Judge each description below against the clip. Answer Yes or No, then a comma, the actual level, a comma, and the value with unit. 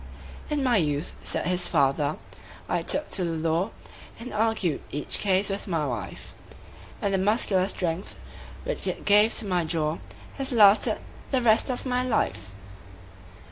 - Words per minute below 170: Yes, average, 155 wpm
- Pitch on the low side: No, high, 195 Hz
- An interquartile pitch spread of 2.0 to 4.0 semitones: No, wide, 5.6 semitones